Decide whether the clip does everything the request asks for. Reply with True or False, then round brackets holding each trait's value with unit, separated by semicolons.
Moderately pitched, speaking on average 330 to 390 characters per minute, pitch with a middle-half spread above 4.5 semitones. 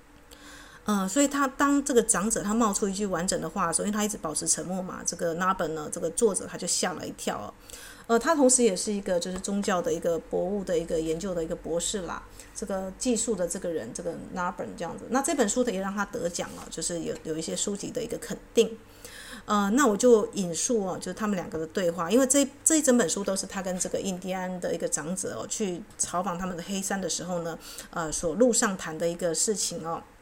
False (195 Hz; 355 characters per minute; 5.1 semitones)